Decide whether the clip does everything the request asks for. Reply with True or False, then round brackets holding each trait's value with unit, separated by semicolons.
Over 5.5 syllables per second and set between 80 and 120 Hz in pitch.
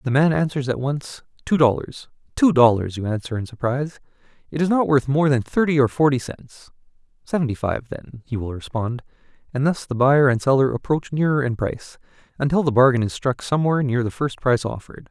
False (5.9 syllables/s; 135 Hz)